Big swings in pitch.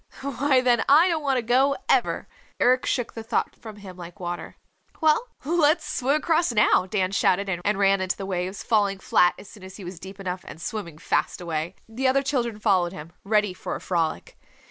Yes: wide, 5.7 semitones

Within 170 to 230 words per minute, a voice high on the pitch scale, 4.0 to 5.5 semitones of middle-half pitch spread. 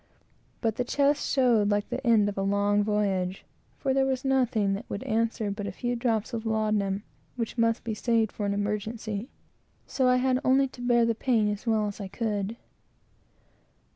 No: average, 190 wpm; high, 220 Hz; average, 3.0 semitones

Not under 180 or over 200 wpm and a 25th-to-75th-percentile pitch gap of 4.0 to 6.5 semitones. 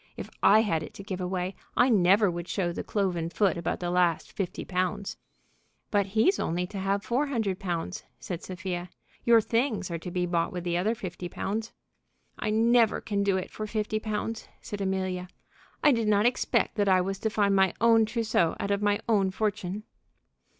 No: average, 195 wpm; average, 3.2 semitones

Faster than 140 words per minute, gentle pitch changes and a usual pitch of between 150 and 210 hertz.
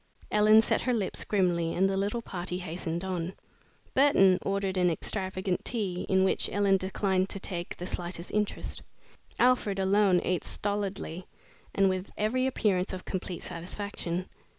Yes: average, 150 wpm; narrow, 2.1 semitones; high, 190 Hz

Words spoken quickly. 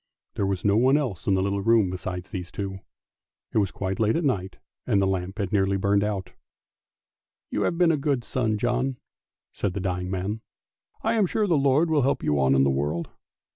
Yes: fast, 220 wpm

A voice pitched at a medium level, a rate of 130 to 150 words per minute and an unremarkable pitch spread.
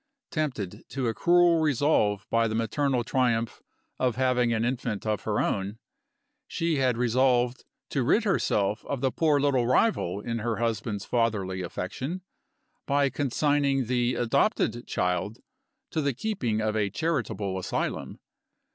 No: low, 120 Hz; average, 140 wpm; average, 4.4 semitones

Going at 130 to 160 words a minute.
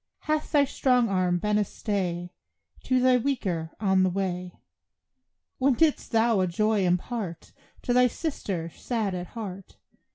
Yes: average, 150 wpm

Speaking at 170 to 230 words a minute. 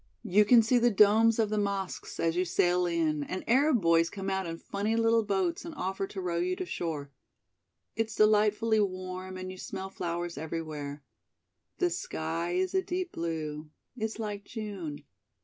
Yes: average, 175 wpm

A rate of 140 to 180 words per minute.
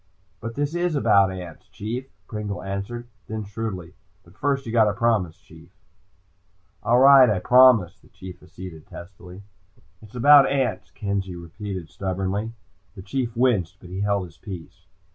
Yes: average, 150 wpm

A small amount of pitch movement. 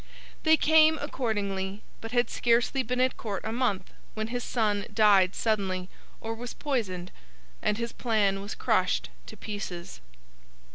No: average, 3.9 semitones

